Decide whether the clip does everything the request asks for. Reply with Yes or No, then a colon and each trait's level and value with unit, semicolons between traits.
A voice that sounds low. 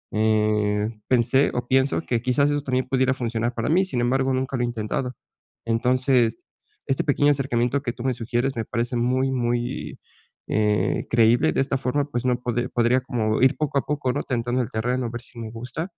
Yes: low, 125 Hz